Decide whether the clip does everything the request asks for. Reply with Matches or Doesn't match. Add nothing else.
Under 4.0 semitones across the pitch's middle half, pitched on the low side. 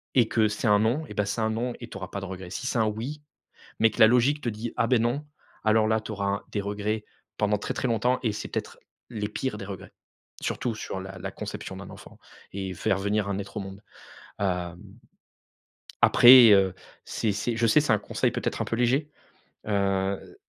Matches